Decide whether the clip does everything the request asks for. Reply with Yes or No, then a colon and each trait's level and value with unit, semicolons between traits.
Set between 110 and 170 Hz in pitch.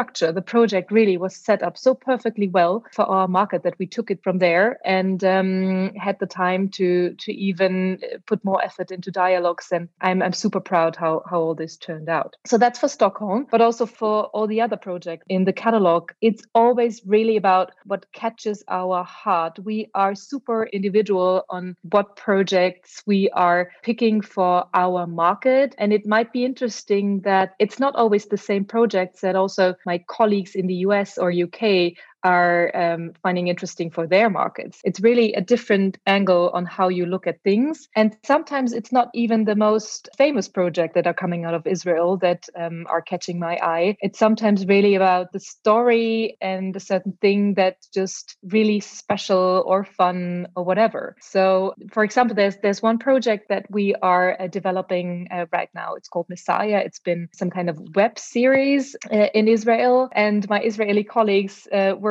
No: high, 195 Hz